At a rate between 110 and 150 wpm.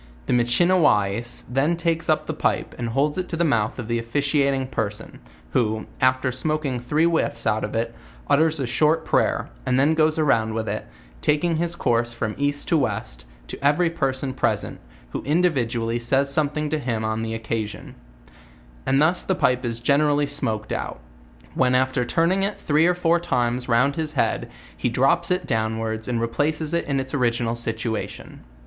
No: average, 180 wpm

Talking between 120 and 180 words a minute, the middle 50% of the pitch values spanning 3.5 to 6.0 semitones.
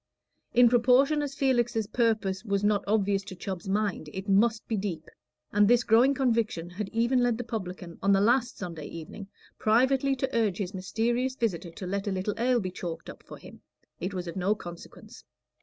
No: average, 190 wpm; average, 4.1 semitones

